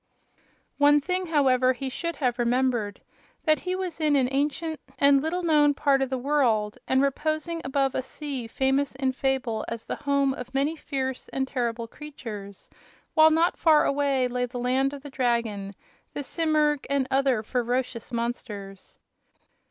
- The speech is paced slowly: No, average, 160 wpm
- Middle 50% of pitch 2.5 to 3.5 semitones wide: Yes, average, 3.0 semitones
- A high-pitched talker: Yes, very high, 270 Hz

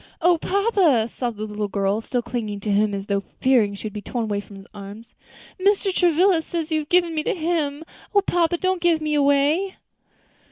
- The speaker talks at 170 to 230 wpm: Yes, average, 200 wpm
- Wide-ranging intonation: Yes, wide, 8.5 semitones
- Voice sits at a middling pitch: No, very high, 285 Hz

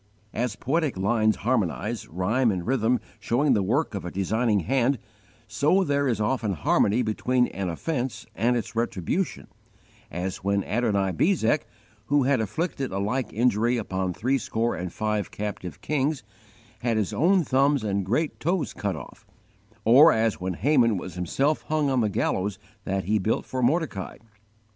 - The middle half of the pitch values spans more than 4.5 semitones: Yes, average, 5.1 semitones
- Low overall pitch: Yes, low, 115 Hz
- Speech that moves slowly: No, average, 155 wpm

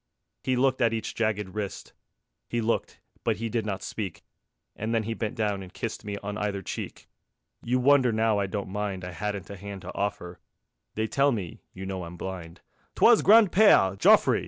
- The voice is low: Yes, low, 105 Hz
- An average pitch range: Yes, average, 3.0 semitones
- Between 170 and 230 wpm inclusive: Yes, average, 195 wpm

